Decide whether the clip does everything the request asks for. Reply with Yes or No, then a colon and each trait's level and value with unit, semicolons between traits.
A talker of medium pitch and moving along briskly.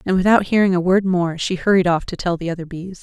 Yes: medium, 180 Hz; fast, 275 wpm